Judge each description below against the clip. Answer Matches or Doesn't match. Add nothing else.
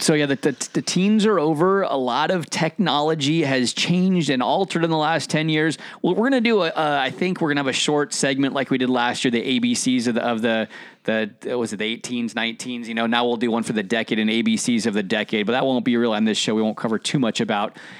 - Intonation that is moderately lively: Doesn't match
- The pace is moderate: Doesn't match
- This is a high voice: Doesn't match